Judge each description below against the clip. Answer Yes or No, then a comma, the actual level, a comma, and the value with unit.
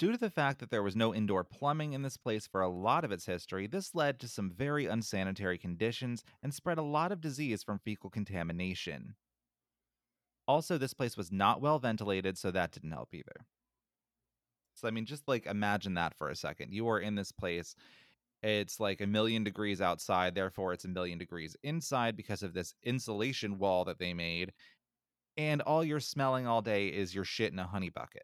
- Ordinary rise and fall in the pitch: No, wide, 5.9 semitones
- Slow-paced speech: No, average, 200 wpm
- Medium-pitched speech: No, low, 105 Hz